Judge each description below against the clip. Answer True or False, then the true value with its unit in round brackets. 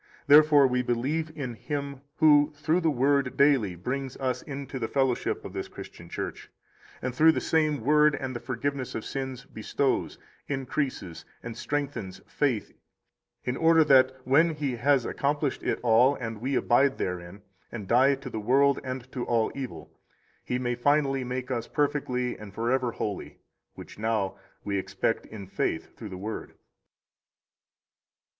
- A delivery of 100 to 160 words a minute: True (155 wpm)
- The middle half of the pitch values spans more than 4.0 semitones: False (3.4 semitones)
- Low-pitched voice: True (130 Hz)